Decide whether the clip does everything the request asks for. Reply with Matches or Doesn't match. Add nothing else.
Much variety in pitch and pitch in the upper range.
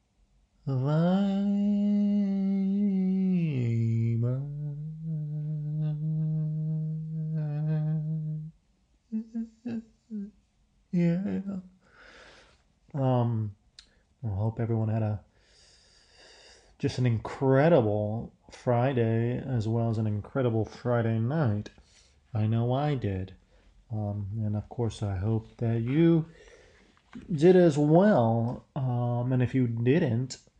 Doesn't match